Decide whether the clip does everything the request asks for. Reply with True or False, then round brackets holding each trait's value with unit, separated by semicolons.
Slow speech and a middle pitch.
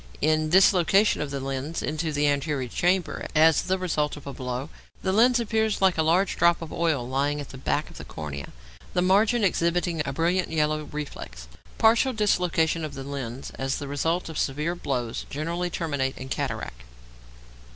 False (180 wpm; 155 Hz)